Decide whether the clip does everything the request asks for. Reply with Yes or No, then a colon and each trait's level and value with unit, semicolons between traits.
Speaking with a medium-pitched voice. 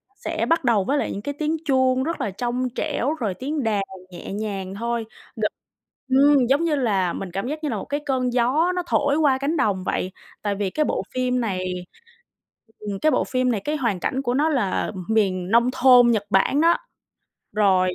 No: high, 245 Hz